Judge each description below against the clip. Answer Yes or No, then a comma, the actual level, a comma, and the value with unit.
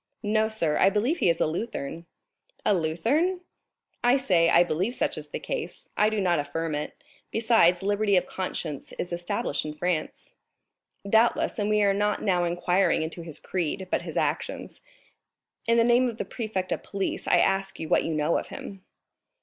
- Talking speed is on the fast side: No, average, 185 wpm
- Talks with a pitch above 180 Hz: Yes, high, 190 Hz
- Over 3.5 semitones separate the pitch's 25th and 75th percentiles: Yes, average, 4.5 semitones